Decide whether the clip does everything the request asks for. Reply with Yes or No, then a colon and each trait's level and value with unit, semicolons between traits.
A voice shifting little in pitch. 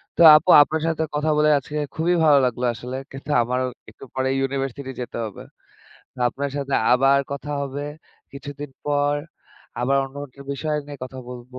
Yes: narrow, 2.1 semitones